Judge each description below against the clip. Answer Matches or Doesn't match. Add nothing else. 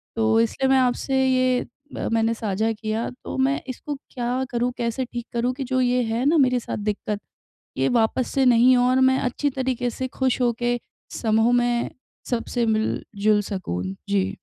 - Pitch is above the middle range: Matches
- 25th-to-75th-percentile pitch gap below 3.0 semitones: Matches